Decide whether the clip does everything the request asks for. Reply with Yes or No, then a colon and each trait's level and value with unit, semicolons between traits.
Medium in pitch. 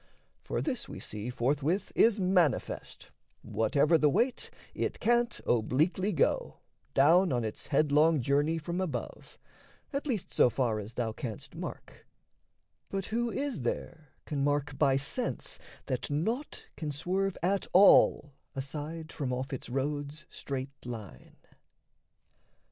Yes: medium, 150 Hz